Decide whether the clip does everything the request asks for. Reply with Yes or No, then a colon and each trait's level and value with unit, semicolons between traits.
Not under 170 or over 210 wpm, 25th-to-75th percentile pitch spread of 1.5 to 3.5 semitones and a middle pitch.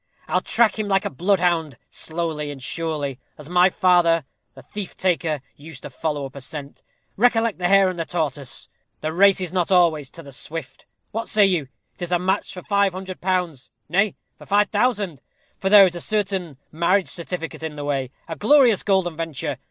No: average, 190 wpm; average, 4.2 semitones; medium, 175 Hz